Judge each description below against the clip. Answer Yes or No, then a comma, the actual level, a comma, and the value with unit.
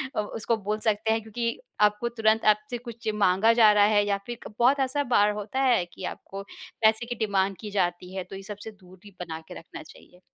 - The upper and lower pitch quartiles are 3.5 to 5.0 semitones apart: No, average, 2.7 semitones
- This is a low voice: No, high, 210 Hz